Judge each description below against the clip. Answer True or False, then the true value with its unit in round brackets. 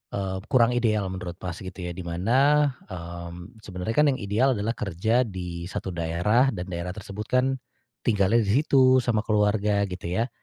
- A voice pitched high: False (100 Hz)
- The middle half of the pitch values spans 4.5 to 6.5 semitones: True (4.9 semitones)